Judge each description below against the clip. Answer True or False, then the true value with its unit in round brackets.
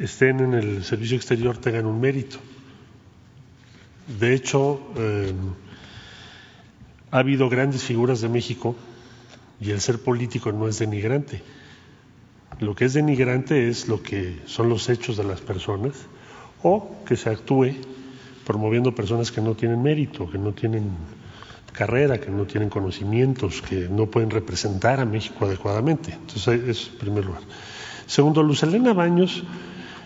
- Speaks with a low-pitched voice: True (120 Hz)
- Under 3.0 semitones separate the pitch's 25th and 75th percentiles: False (3.6 semitones)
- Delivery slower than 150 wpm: True (140 wpm)